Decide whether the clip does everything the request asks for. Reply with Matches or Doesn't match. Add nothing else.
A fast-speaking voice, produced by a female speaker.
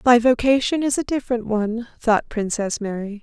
Doesn't match